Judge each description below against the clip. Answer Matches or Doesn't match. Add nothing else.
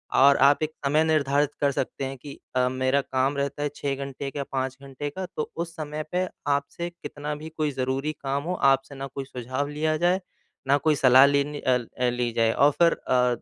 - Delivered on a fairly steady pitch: Matches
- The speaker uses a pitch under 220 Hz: Matches